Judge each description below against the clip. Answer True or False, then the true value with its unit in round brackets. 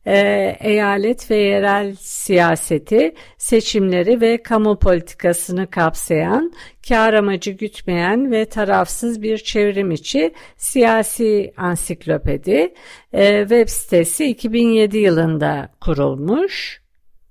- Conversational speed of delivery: False (85 wpm)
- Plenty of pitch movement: False (4.0 semitones)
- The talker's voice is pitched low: False (205 Hz)